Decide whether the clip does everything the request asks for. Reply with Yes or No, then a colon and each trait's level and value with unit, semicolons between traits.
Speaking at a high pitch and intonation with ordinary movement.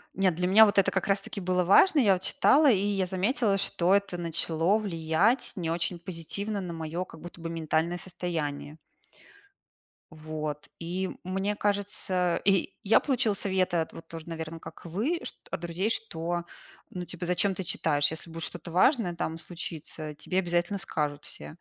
No: medium, 175 Hz; average, 3.2 semitones